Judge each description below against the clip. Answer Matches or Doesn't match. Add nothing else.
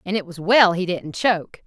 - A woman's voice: Matches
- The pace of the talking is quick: Matches